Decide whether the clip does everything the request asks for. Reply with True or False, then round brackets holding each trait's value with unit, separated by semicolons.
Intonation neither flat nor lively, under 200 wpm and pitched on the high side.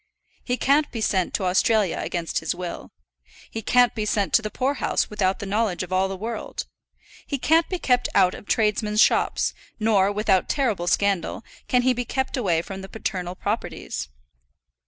True (4.3 semitones; 180 wpm; 210 Hz)